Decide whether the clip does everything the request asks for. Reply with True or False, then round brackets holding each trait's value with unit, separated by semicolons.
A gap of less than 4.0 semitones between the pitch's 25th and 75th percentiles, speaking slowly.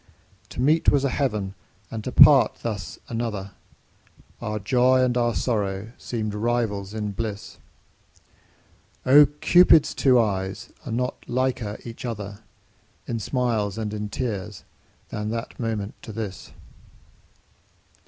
True (3.3 semitones; 125 wpm)